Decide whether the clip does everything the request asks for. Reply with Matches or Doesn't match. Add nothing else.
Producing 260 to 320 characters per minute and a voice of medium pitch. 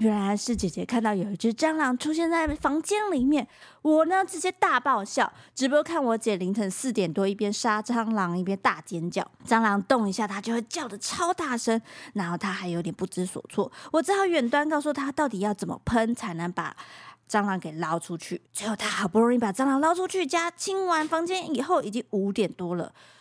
Doesn't match